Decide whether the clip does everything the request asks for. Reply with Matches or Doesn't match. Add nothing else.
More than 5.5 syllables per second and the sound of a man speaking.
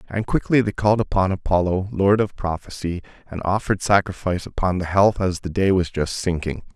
Matches